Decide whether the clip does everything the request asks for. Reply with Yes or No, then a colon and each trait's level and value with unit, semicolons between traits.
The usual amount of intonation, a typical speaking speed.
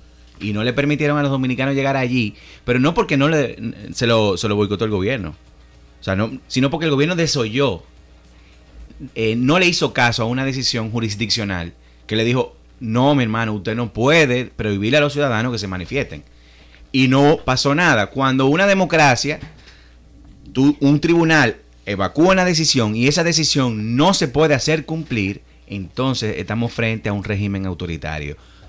No: wide, 6.3 semitones; average, 170 wpm